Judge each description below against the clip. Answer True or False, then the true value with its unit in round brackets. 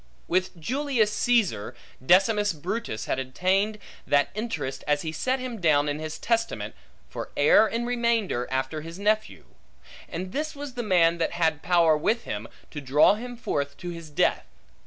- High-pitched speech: False (180 Hz)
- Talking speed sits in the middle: True (165 wpm)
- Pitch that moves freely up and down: True (7.4 semitones)